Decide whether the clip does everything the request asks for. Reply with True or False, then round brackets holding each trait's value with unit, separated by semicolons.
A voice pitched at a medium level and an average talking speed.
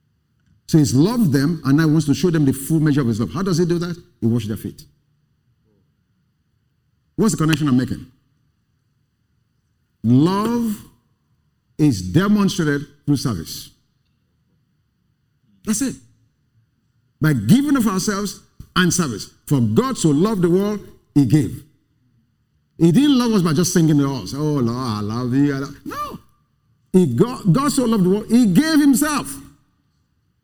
True (150 Hz; 150 wpm)